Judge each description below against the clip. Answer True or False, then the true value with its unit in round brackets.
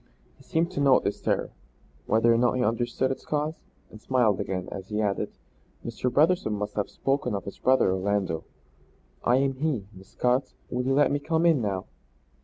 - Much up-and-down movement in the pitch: False (5.0 semitones)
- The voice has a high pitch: False (125 Hz)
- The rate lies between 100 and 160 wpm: False (195 wpm)